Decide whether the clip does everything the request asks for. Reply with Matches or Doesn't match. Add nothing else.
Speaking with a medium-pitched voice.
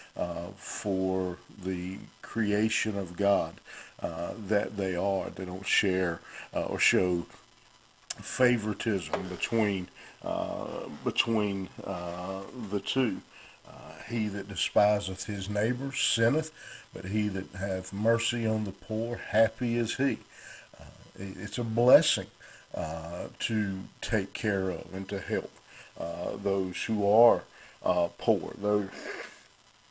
Doesn't match